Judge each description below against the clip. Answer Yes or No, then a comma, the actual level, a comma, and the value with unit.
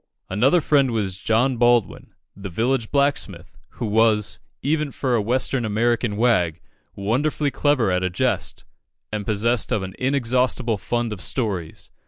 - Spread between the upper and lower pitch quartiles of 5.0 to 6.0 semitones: No, average, 3.9 semitones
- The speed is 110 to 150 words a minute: Yes, average, 145 wpm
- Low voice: Yes, low, 115 Hz